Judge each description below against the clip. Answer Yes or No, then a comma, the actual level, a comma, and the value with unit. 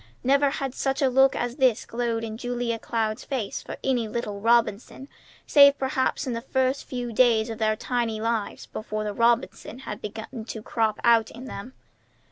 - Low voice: No, high, 235 Hz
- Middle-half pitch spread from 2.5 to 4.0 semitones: Yes, average, 2.9 semitones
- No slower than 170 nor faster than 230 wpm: Yes, average, 180 wpm